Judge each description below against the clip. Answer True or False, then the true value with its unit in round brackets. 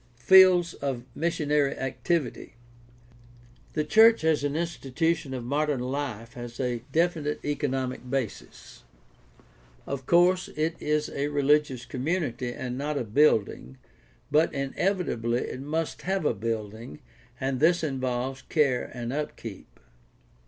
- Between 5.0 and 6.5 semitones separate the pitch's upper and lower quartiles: False (4.1 semitones)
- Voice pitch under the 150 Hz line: True (140 Hz)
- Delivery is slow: True (120 wpm)